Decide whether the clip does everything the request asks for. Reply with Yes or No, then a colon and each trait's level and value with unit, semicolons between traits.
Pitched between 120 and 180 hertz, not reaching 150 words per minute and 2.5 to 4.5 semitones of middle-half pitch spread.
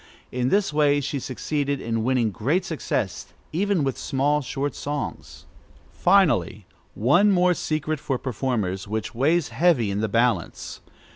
No: low, 135 Hz; average, 140 wpm; wide, 5.4 semitones